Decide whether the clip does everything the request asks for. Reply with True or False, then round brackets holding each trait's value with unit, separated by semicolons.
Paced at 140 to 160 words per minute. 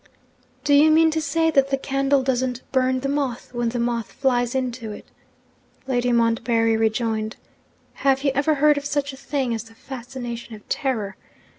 False (175 wpm)